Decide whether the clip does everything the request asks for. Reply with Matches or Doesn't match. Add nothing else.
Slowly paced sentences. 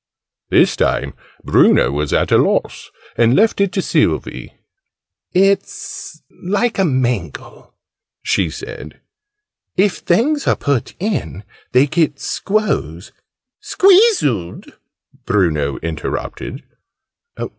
Matches